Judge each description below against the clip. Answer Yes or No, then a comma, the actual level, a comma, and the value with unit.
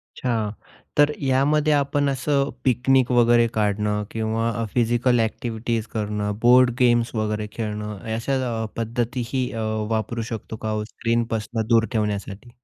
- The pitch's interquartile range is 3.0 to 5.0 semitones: No, narrow, 2.5 semitones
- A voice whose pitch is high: No, low, 115 Hz